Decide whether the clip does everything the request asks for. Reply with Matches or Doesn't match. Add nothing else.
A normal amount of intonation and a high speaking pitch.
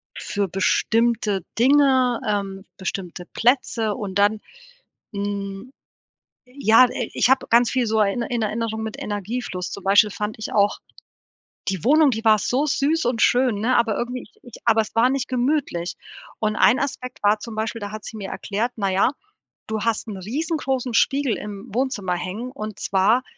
Matches